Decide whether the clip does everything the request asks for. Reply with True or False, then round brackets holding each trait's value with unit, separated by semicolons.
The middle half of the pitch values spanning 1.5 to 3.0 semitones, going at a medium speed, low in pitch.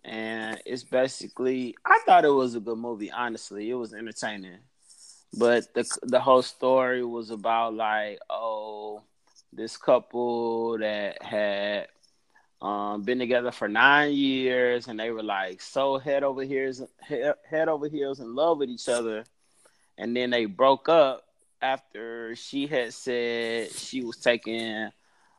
True (2.7 semitones; 145 wpm; 120 Hz)